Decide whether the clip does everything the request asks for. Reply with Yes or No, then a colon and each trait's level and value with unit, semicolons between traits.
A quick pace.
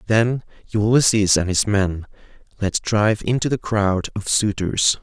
No: average, 145 wpm